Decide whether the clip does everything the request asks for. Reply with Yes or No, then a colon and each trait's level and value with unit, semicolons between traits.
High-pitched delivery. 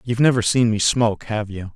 No: low, 110 Hz